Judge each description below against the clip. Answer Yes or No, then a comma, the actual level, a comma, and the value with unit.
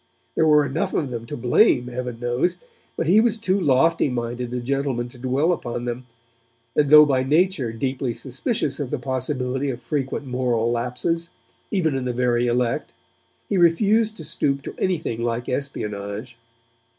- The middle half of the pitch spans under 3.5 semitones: No, average, 3.9 semitones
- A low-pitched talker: Yes, low, 130 Hz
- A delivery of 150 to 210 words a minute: Yes, average, 165 wpm